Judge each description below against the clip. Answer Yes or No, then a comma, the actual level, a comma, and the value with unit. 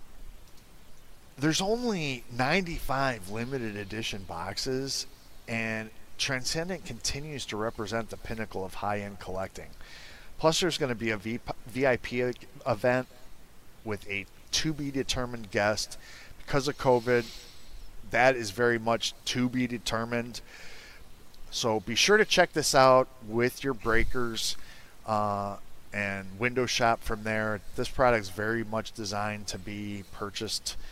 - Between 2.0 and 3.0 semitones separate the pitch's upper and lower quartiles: No, average, 3.8 semitones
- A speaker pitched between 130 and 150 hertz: No, low, 115 Hz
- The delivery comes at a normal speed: No, slow, 120 wpm